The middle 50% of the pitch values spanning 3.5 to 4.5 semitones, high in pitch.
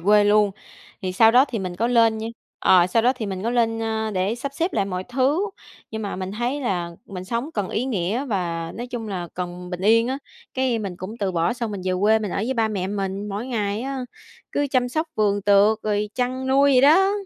Yes: average, 4.2 semitones; high, 220 Hz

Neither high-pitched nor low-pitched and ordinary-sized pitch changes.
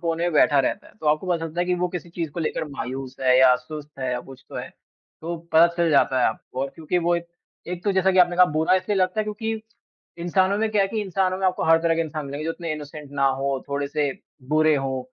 Yes: medium, 165 Hz; average, 4.3 semitones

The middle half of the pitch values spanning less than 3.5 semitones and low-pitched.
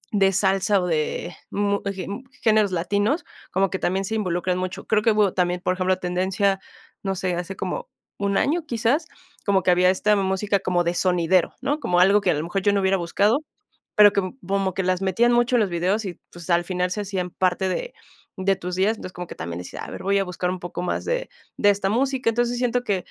No: narrow, 2.5 semitones; high, 195 Hz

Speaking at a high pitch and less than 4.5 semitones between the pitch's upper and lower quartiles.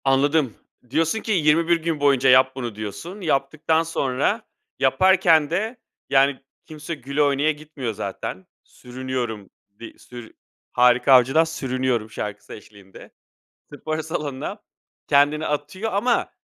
No: medium, 140 Hz; average, 4.0 semitones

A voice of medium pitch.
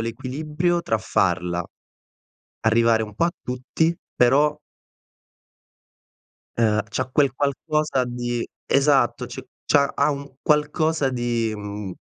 No: low, 125 Hz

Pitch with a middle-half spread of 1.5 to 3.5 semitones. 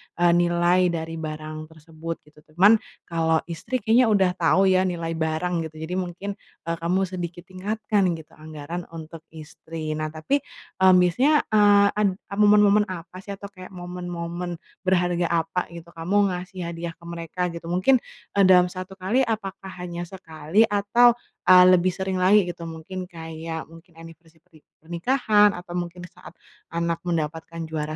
Yes: narrow, 2.5 semitones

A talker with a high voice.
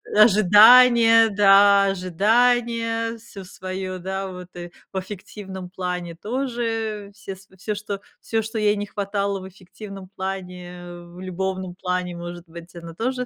Yes: high, 195 Hz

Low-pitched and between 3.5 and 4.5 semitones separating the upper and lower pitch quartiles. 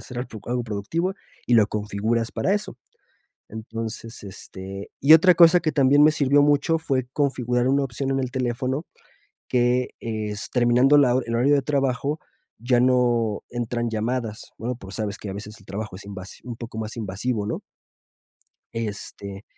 Yes: low, 120 Hz; average, 3.9 semitones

